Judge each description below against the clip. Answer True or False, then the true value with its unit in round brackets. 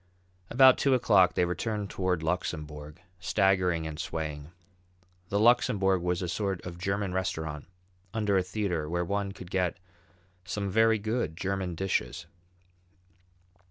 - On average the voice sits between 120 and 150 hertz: False (95 Hz)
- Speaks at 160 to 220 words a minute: False (135 wpm)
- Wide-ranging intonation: False (3.0 semitones)